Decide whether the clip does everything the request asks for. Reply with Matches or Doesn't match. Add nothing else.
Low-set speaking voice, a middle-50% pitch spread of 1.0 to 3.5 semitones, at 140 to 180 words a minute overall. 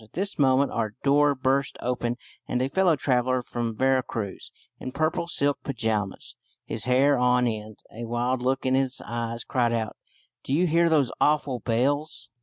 Matches